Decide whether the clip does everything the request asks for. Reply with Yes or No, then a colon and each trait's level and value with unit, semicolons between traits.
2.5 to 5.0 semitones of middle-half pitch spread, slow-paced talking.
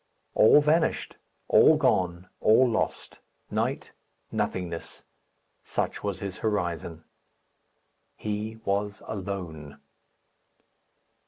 Yes: average, 3.7 semitones; slow, 80 wpm